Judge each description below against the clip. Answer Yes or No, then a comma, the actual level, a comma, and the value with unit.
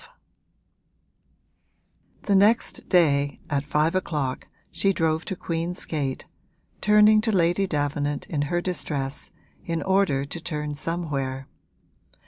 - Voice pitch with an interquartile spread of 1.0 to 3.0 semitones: No, average, 4.2 semitones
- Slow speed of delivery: Yes, slow, 115 wpm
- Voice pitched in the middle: Yes, medium, 160 Hz